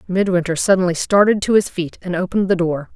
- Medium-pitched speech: Yes, medium, 180 Hz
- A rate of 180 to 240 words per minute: Yes, fast, 205 wpm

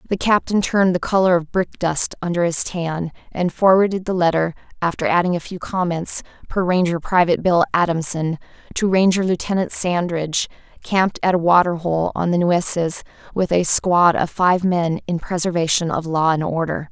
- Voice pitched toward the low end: No, medium, 175 Hz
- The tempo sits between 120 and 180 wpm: Yes, average, 175 wpm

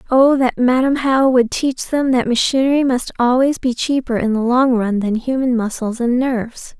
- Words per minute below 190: No, average, 195 wpm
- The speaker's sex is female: Yes, female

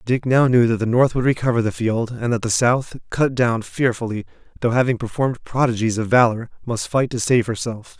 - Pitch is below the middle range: Yes, low, 120 Hz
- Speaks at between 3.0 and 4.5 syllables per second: No, 5.4 syllables/s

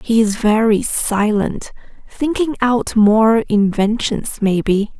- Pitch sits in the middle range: No, high, 220 Hz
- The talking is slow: Yes, slow, 95 wpm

